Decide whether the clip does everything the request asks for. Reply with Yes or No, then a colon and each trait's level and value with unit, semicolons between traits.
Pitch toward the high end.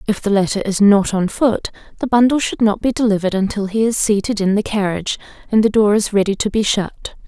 Yes: high, 210 Hz